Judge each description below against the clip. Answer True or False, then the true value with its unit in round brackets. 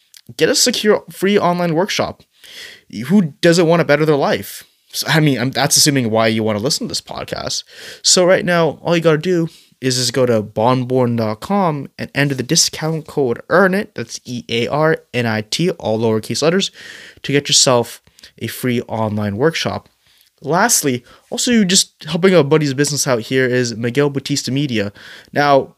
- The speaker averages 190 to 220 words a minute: False (180 wpm)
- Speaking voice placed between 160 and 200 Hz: False (140 Hz)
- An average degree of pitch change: False (5.8 semitones)